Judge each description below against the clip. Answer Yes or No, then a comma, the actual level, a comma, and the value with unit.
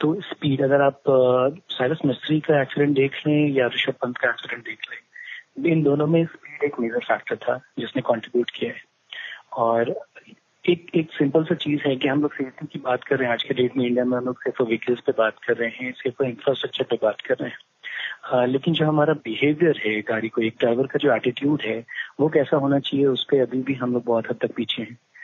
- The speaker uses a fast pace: Yes, fast, 230 wpm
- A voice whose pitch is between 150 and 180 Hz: No, low, 135 Hz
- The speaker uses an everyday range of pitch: Yes, average, 3.4 semitones